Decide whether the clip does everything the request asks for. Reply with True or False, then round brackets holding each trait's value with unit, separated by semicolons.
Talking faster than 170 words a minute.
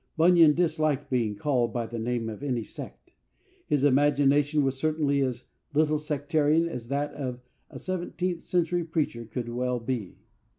False (155 wpm)